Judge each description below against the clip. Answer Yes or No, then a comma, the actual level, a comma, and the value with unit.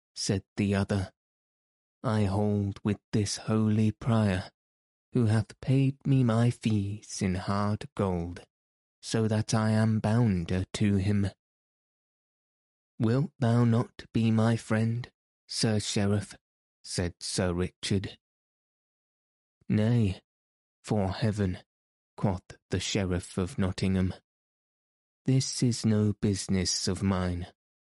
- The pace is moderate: No, slow, 110 wpm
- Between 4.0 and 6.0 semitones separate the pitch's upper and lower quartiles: No, average, 3.1 semitones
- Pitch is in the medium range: No, low, 105 Hz